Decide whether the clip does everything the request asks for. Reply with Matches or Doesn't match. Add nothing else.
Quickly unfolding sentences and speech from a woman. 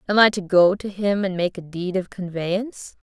Matches